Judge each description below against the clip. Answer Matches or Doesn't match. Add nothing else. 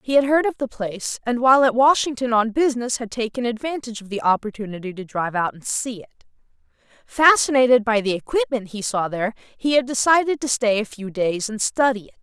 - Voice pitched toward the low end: Doesn't match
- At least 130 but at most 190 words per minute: Doesn't match